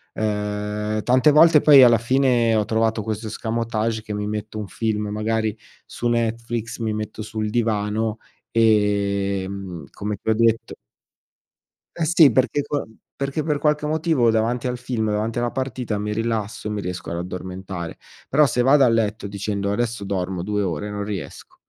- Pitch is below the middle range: Yes, low, 110 Hz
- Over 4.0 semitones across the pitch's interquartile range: No, narrow, 2.5 semitones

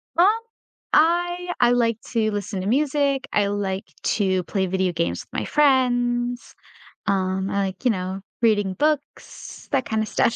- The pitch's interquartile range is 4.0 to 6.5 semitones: Yes, wide, 5.5 semitones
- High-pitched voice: Yes, high, 225 Hz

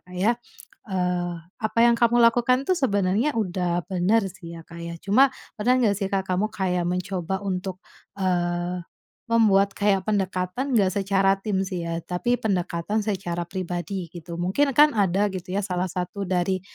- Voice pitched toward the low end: No, high, 190 Hz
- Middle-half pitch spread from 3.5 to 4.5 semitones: No, average, 3.0 semitones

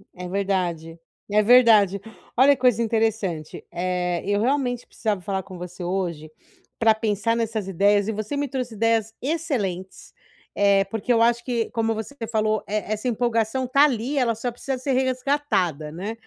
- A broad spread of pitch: No, average, 4.1 semitones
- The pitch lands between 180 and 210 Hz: No, high, 220 Hz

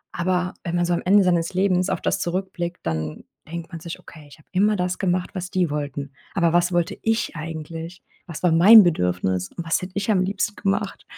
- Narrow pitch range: Yes, narrow, 2.2 semitones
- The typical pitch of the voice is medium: Yes, medium, 175 Hz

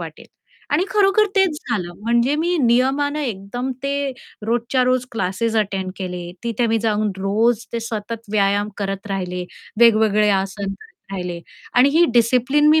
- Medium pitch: No, high, 230 Hz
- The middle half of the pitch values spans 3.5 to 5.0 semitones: Yes, average, 4.5 semitones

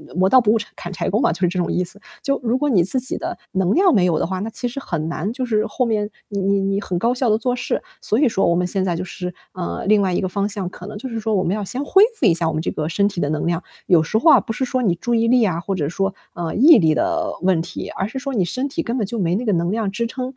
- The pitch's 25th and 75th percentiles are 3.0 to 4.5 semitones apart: No, average, 5.2 semitones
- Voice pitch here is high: Yes, high, 205 Hz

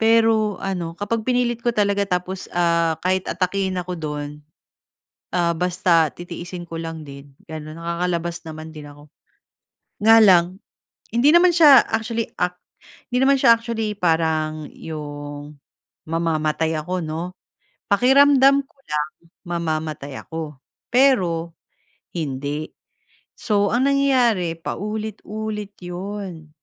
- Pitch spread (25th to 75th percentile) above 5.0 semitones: Yes, wide, 5.4 semitones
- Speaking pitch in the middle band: Yes, medium, 180 Hz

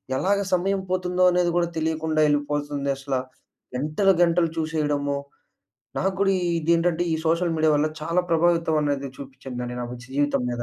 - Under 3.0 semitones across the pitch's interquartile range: No, average, 3.3 semitones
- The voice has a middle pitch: Yes, medium, 160 Hz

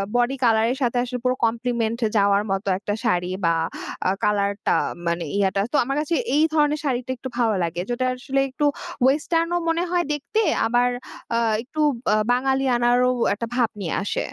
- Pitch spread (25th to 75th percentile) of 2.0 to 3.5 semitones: No, average, 4.5 semitones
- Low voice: No, high, 245 Hz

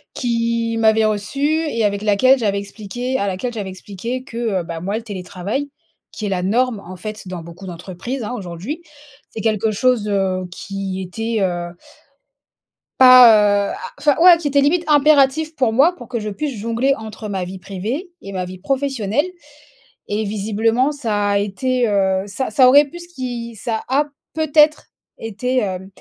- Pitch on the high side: Yes, high, 220 Hz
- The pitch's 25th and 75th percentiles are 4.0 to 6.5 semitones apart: Yes, average, 4.7 semitones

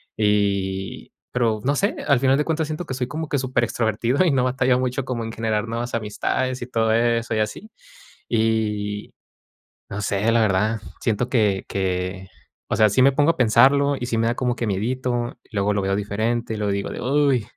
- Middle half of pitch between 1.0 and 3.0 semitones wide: No, average, 3.5 semitones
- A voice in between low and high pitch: No, low, 115 Hz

